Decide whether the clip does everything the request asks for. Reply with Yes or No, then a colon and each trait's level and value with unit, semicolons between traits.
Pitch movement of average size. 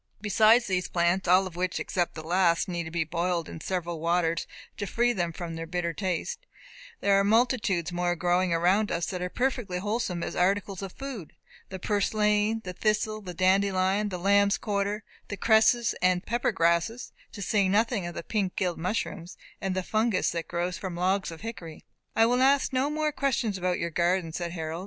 Yes: average, 3.6 semitones